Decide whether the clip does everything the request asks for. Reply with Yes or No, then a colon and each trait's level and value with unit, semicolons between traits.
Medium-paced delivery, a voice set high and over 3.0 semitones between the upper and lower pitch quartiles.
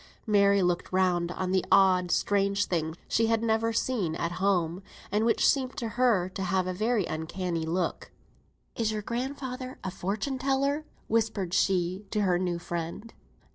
Yes: average, 165 wpm; high, 195 Hz; average, 4.2 semitones